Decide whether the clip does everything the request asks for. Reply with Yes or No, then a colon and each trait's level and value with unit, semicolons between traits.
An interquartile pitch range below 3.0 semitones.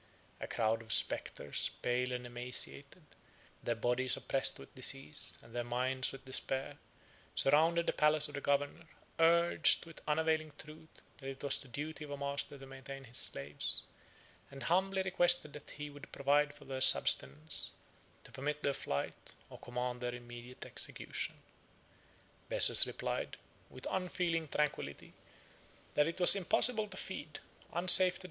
No: average, 3.5 semitones